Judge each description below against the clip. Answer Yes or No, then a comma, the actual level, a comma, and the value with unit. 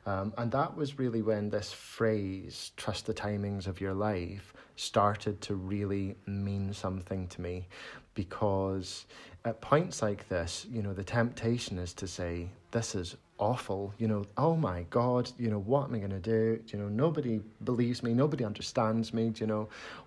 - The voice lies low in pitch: Yes, low, 105 Hz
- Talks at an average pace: Yes, average, 180 wpm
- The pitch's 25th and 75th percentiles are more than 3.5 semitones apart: No, average, 3.0 semitones